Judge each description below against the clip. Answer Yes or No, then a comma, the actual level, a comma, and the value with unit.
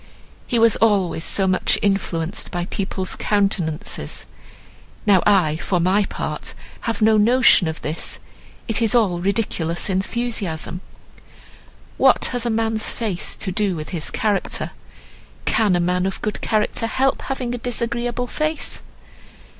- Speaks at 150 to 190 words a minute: No, average, 140 wpm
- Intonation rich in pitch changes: No, average, 4.0 semitones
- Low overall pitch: No, high, 205 Hz